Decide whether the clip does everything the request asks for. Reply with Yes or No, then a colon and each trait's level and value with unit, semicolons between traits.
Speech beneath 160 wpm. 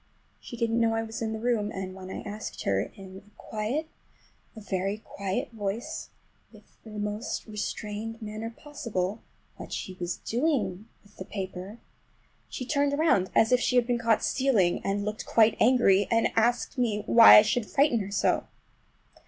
No: average, 170 wpm